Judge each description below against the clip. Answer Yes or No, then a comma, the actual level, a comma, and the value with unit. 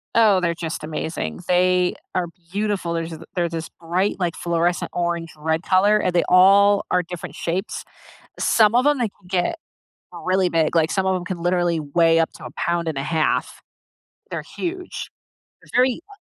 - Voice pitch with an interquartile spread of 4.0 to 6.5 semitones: No, average, 2.8 semitones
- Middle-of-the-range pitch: Yes, medium, 175 Hz